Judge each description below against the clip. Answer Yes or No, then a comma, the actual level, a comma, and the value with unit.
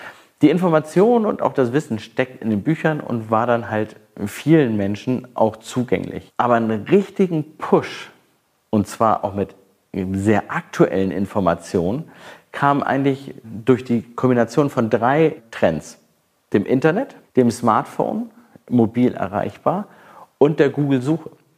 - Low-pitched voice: Yes, low, 125 Hz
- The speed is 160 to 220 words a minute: No, average, 130 wpm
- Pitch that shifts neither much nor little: No, wide, 6.1 semitones